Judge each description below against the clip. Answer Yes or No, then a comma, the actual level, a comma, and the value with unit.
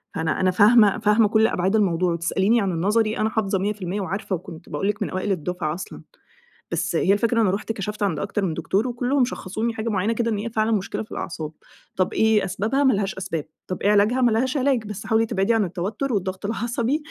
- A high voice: Yes, high, 210 Hz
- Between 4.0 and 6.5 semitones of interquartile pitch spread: No, average, 3.1 semitones